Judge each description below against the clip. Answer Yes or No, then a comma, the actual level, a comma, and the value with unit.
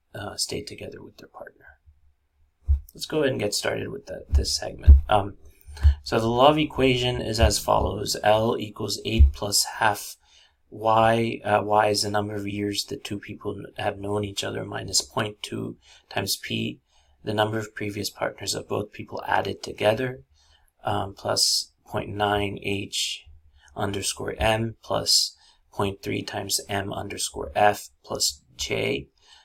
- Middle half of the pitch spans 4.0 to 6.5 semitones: Yes, average, 5.1 semitones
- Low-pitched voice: Yes, low, 100 Hz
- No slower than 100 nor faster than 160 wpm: Yes, average, 145 wpm